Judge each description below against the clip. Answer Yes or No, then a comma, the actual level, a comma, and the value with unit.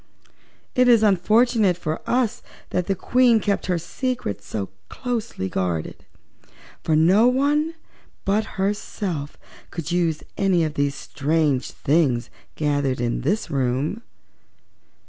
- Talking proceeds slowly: Yes, slow, 120 wpm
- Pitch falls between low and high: Yes, medium, 175 Hz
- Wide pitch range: Yes, wide, 7.3 semitones